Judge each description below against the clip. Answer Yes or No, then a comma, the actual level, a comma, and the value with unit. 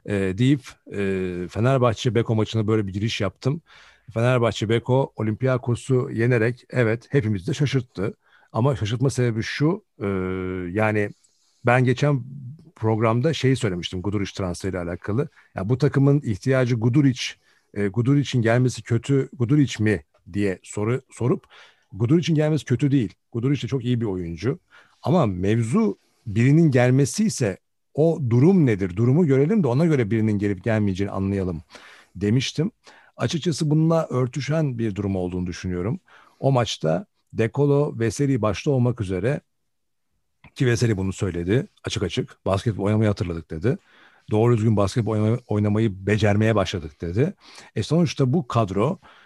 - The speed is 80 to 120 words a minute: No, average, 135 wpm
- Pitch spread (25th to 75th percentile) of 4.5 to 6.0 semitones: Yes, average, 4.9 semitones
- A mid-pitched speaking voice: No, low, 115 Hz